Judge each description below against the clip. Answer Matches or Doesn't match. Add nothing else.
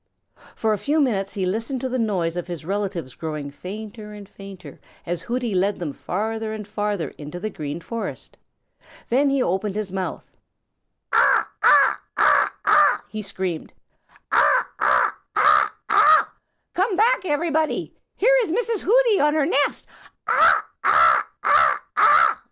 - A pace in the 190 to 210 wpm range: Doesn't match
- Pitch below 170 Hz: Doesn't match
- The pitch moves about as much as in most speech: Doesn't match